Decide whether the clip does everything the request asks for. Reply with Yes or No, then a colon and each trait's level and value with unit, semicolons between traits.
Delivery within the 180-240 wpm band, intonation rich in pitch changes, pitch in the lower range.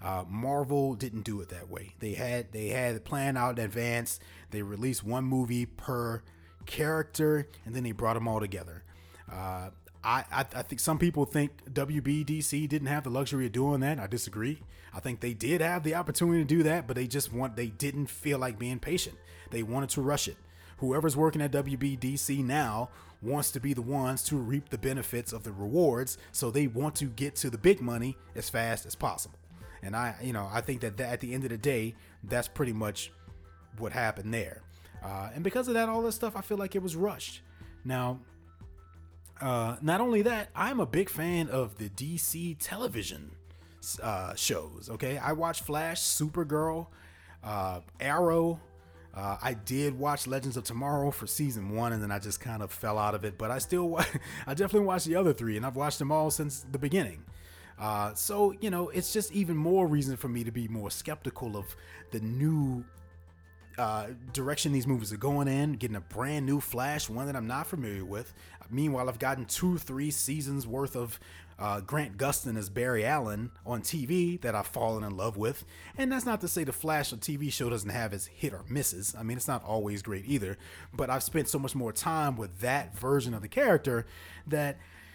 Yes: fast, 205 wpm; wide, 5.9 semitones; low, 125 Hz